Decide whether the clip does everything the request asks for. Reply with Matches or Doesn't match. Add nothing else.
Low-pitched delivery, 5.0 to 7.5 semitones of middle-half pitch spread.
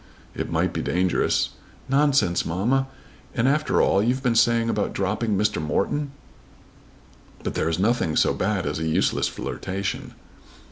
Matches